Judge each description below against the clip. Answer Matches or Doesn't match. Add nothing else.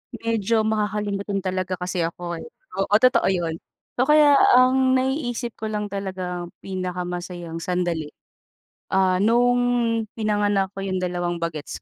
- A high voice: Matches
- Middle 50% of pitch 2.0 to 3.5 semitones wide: Doesn't match